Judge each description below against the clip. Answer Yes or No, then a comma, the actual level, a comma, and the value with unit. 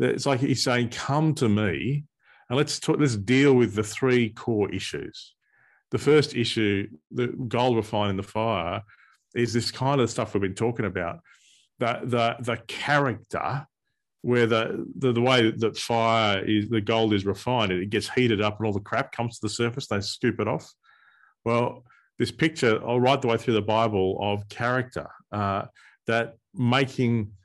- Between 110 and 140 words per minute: No, average, 180 wpm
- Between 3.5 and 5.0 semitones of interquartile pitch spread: No, average, 3.1 semitones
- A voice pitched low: Yes, low, 115 Hz